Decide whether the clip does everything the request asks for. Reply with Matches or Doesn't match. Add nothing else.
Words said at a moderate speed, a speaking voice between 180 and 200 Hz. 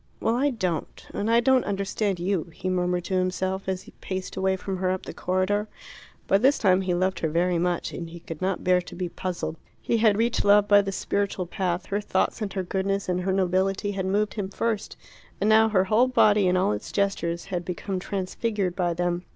Doesn't match